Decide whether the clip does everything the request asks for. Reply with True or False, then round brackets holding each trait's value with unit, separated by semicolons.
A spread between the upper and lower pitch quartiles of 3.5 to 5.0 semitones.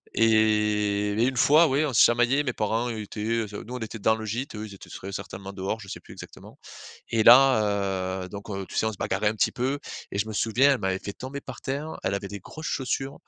True (3.8 semitones)